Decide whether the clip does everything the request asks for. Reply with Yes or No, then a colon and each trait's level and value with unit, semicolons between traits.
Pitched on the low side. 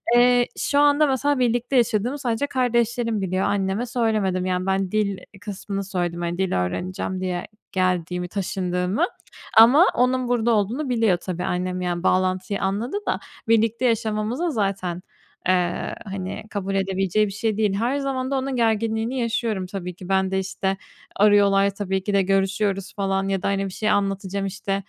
No: high, 200 Hz